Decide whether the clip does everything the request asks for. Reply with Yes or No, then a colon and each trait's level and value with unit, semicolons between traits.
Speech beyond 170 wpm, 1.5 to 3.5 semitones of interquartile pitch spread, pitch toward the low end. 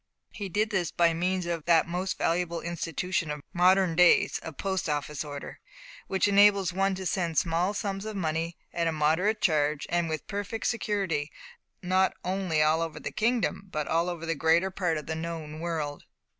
No: average, 180 wpm; average, 2.9 semitones; medium, 170 Hz